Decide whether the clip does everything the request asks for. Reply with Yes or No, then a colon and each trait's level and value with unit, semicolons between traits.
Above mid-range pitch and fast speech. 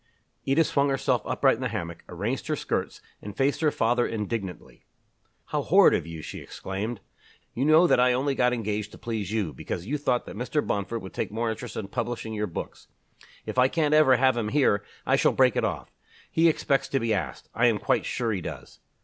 No: low, 120 Hz; fast, 215 wpm